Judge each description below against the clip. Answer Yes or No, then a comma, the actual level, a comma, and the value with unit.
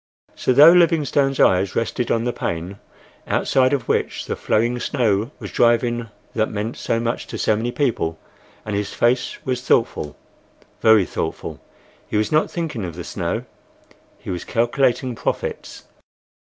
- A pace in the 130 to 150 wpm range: Yes, average, 145 wpm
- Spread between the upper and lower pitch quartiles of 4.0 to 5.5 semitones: No, average, 3.4 semitones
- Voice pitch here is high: No, low, 120 Hz